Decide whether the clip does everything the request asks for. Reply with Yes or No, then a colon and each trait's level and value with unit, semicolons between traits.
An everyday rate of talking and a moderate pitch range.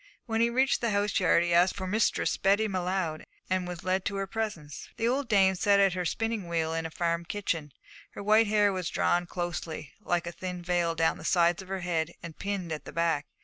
No: fast, 230 wpm; average, 3.1 semitones